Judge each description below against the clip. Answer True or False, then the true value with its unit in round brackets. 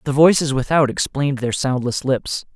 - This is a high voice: False (135 Hz)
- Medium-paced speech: True (165 wpm)